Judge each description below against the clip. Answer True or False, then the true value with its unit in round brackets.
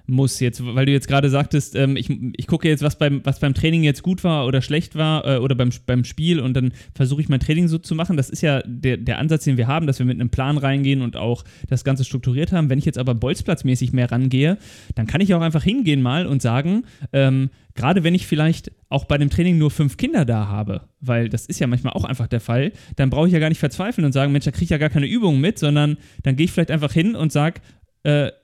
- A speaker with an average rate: False (265 wpm)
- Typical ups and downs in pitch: True (3.7 semitones)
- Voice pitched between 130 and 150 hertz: True (140 Hz)